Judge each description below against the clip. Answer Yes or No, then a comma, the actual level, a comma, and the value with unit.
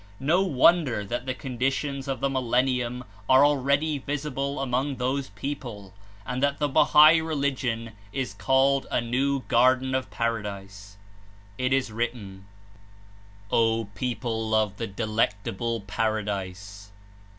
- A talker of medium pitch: No, low, 125 Hz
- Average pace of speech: No, slow, 130 wpm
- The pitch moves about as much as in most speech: Yes, average, 3.9 semitones